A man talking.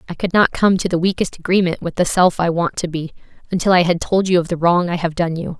No: female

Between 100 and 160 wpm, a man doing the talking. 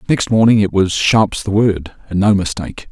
No: fast, 205 wpm; male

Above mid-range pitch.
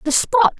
Yes: very high, 315 Hz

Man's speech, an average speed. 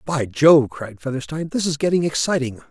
Yes: male; average, 180 wpm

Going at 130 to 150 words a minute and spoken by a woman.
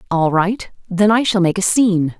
No: fast, 220 wpm; female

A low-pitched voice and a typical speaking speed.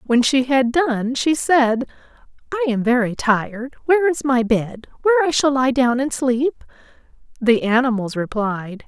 No: very high, 255 Hz; average, 160 wpm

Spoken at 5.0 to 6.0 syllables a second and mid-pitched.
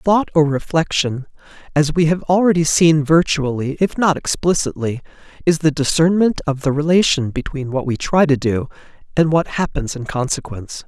Yes: 5.1 syllables/s; medium, 155 Hz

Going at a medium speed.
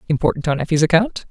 Yes: average, 185 wpm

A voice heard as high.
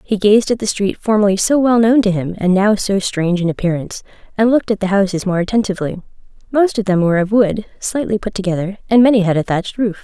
Yes: high, 205 Hz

